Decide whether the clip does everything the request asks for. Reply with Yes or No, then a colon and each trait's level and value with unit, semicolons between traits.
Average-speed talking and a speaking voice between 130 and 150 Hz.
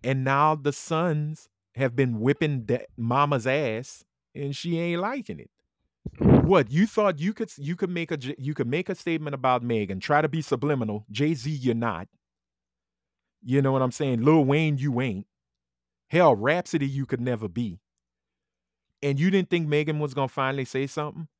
Yes: average, 180 wpm; medium, 140 Hz